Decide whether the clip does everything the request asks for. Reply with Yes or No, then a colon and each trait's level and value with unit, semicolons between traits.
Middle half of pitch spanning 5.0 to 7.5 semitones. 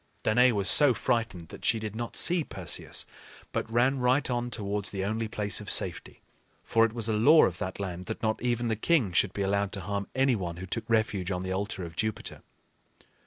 No: average, 3.3 semitones